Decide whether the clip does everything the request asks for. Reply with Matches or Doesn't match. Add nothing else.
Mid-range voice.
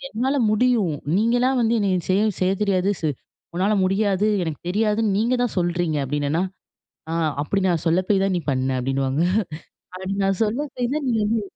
Doesn't match